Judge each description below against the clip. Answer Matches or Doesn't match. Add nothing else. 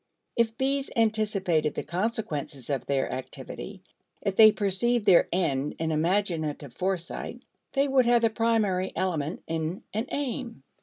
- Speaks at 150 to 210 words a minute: Doesn't match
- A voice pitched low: Doesn't match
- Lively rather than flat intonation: Matches